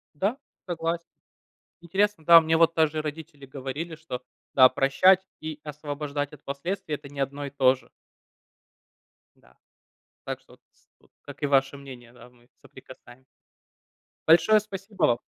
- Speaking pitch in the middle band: Yes, medium, 150 Hz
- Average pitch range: Yes, average, 3.5 semitones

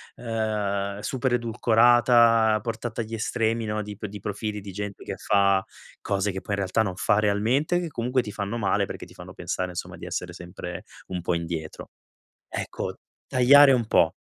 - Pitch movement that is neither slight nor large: Yes, average, 3.0 semitones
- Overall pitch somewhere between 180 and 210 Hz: No, low, 105 Hz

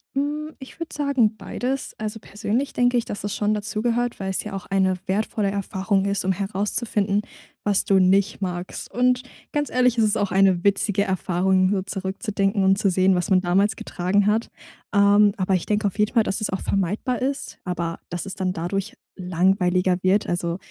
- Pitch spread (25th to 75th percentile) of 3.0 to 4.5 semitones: No, narrow, 2.4 semitones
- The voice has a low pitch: No, high, 200 Hz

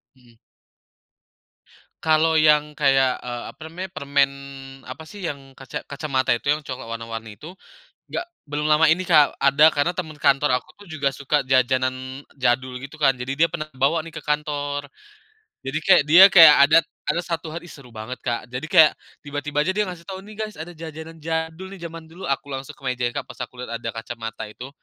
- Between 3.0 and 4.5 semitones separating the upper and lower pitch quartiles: Yes, average, 3.7 semitones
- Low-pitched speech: No, medium, 145 Hz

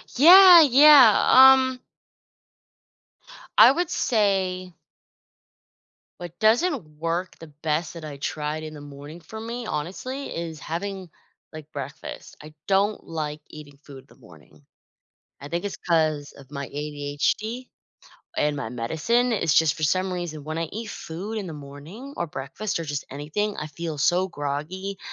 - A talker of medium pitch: Yes, medium, 165 Hz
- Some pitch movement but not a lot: No, wide, 6.2 semitones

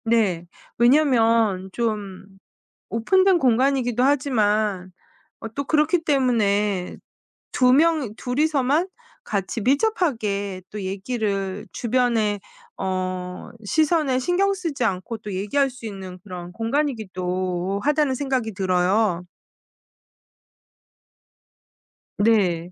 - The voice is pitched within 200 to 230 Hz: Yes, high, 225 Hz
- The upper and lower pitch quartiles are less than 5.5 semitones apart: No, wide, 6.0 semitones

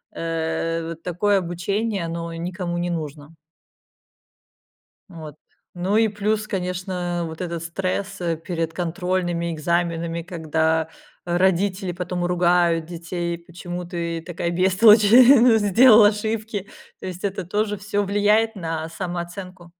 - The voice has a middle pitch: Yes, medium, 175 Hz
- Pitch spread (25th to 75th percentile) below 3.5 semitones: Yes, average, 2.9 semitones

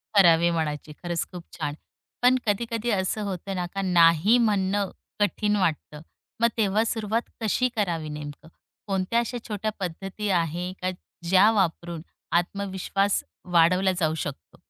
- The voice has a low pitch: No, high, 190 Hz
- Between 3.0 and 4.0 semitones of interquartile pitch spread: Yes, average, 3.7 semitones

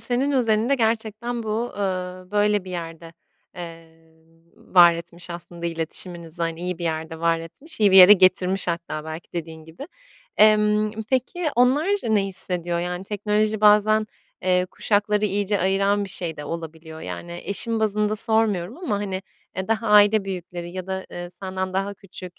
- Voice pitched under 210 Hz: Yes, high, 190 Hz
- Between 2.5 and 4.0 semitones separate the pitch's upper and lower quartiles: Yes, average, 3.7 semitones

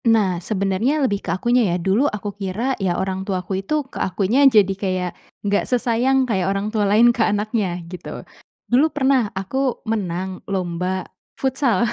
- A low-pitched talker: No, high, 205 Hz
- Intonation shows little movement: No, average, 4.0 semitones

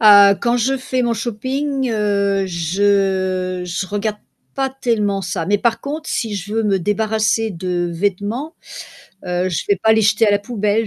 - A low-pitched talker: No, high, 205 Hz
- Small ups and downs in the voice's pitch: No, average, 3.1 semitones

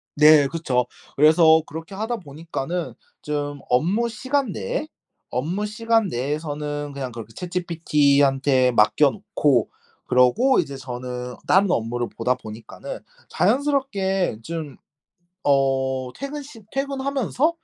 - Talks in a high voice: No, medium, 150 Hz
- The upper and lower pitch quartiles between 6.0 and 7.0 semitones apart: No, wide, 7.6 semitones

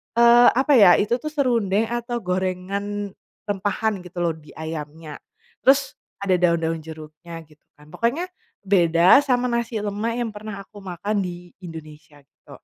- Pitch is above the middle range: Yes, high, 195 Hz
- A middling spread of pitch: No, wide, 5.8 semitones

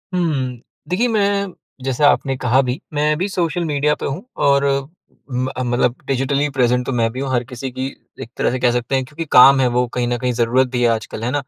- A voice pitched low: Yes, low, 130 Hz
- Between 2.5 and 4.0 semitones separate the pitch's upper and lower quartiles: Yes, average, 3.0 semitones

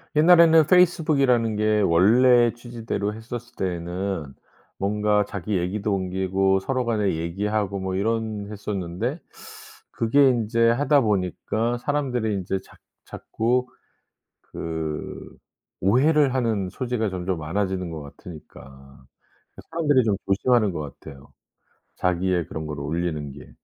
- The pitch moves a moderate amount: Yes, average, 4.9 semitones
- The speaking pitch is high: No, low, 105 Hz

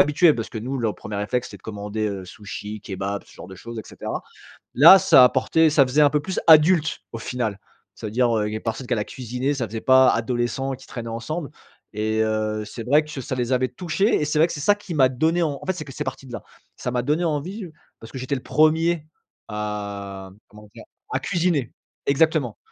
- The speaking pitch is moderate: No, low, 125 Hz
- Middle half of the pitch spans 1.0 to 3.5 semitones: No, wide, 5.6 semitones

